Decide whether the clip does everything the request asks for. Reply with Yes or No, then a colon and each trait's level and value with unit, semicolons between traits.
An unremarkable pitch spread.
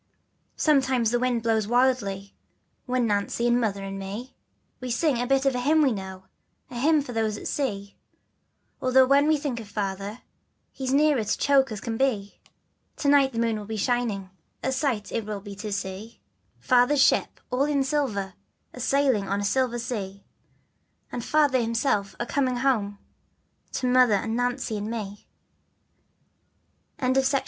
Yes: average, 4.4 semitones